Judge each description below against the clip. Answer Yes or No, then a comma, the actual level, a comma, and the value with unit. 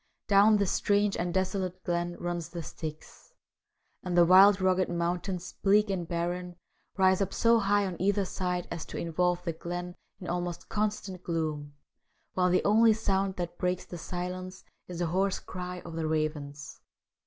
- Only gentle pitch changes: Yes, narrow, 2.0 semitones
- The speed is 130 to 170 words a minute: Yes, average, 165 wpm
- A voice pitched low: No, medium, 180 Hz